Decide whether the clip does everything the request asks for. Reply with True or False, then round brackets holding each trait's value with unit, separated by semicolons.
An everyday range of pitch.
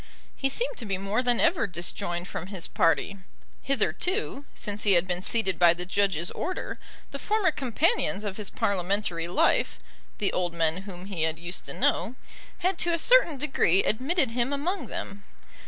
False (7.9 semitones)